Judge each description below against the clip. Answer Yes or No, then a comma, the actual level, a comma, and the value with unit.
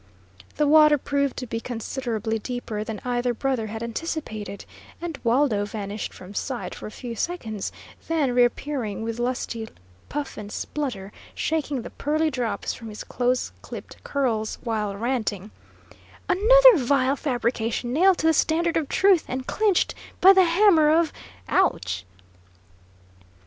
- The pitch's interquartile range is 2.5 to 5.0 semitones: No, wide, 5.6 semitones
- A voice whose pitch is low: No, very high, 255 Hz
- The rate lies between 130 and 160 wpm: Yes, average, 140 wpm